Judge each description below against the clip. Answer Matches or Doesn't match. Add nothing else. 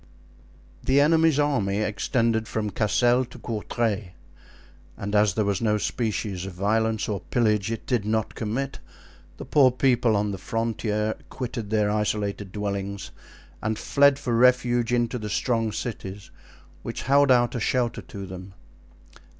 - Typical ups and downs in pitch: Matches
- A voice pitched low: Matches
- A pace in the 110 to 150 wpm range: Matches